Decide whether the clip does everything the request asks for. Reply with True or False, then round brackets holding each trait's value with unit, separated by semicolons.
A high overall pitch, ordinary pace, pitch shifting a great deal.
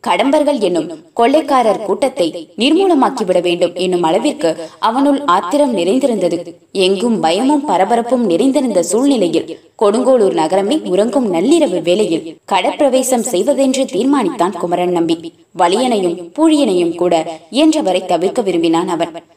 True (205 Hz; 100 wpm; 8.2 semitones)